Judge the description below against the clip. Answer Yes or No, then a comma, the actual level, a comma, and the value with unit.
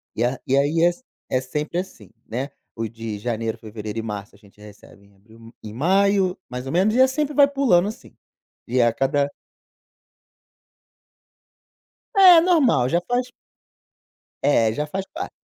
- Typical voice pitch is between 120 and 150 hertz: Yes, low, 135 Hz